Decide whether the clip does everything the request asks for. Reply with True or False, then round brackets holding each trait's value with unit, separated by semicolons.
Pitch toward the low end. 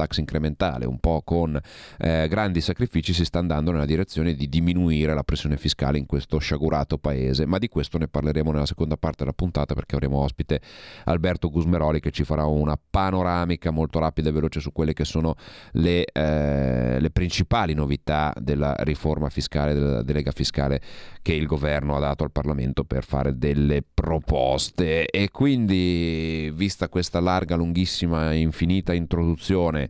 True (80 Hz)